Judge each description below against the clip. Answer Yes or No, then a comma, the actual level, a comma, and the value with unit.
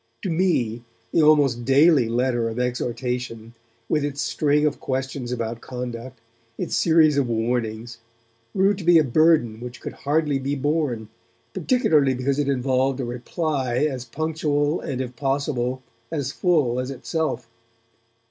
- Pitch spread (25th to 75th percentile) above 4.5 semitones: No, average, 3.7 semitones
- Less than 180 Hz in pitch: Yes, low, 135 Hz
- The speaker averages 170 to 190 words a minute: No, average, 145 wpm